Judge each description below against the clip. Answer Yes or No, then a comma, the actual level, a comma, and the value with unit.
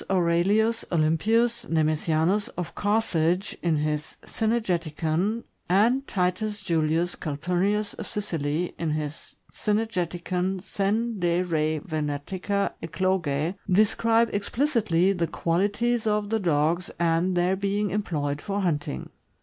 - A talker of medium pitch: Yes, medium, 180 Hz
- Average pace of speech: No, slow, 115 wpm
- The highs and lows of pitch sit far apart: No, average, 4.3 semitones